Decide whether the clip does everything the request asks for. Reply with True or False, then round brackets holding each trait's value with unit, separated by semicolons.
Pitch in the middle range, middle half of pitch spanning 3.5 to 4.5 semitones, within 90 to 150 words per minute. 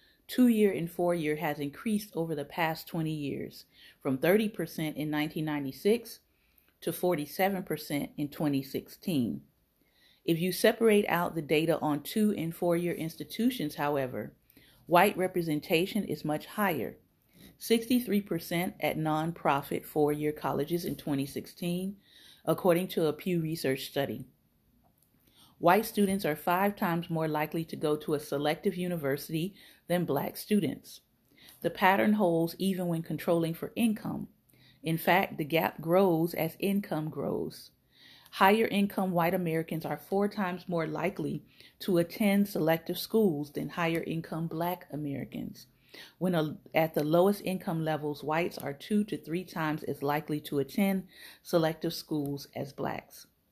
True (165 Hz; 3.8 semitones; 140 wpm)